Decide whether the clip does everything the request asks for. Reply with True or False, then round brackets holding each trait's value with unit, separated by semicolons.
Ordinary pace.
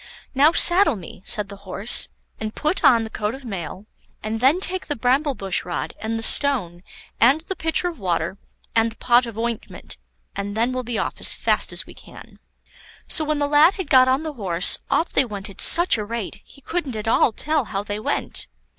False (215 wpm)